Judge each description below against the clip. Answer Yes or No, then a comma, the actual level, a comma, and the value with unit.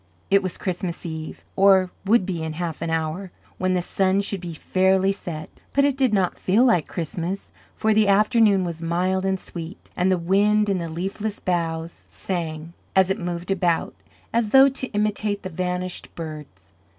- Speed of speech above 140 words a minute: Yes, average, 180 wpm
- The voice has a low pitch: No, medium, 185 Hz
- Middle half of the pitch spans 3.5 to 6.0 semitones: No, average, 2.9 semitones